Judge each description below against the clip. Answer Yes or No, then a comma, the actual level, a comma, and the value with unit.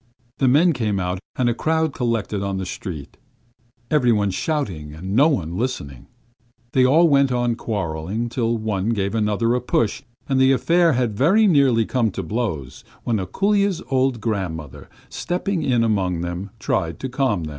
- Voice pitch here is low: Yes, low, 115 Hz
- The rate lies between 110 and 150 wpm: No, average, 170 wpm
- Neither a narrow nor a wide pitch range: No, wide, 5.9 semitones